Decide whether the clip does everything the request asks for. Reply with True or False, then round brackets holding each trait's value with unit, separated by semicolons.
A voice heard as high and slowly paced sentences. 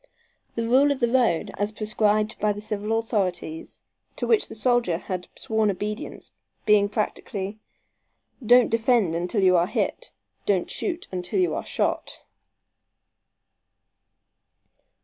True (215 Hz; 130 wpm)